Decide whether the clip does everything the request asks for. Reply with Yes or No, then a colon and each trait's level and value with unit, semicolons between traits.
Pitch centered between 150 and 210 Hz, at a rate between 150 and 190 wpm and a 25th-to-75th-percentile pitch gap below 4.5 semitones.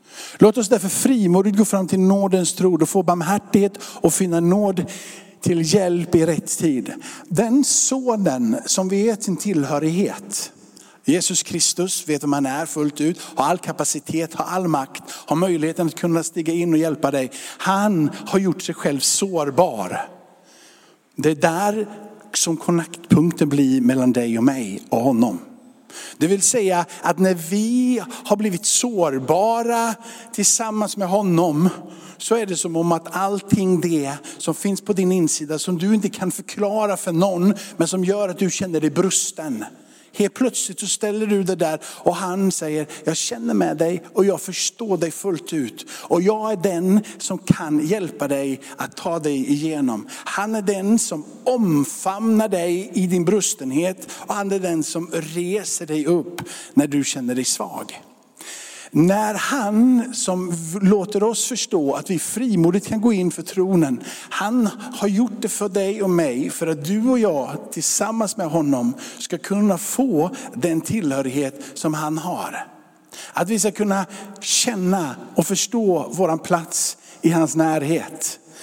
Yes: medium, 185 Hz; average, 160 wpm; average, 4.0 semitones